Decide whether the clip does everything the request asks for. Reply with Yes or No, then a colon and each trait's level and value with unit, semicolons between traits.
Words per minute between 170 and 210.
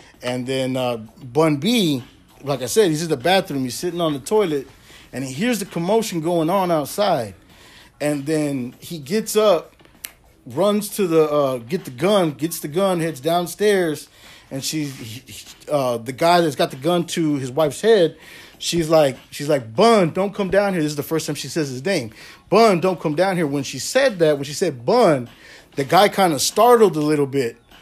Yes: fast, 205 wpm